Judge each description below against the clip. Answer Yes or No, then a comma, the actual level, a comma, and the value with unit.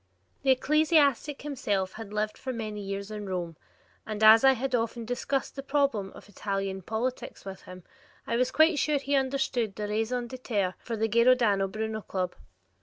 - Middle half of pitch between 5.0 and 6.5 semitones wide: No, average, 4.5 semitones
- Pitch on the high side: Yes, high, 225 Hz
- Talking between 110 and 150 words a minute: No, average, 170 wpm